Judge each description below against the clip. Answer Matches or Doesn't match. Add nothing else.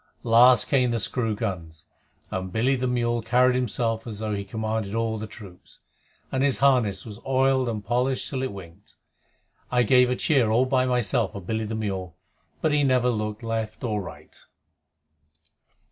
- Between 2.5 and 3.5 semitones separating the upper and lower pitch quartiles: Matches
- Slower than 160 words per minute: Doesn't match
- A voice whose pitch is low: Matches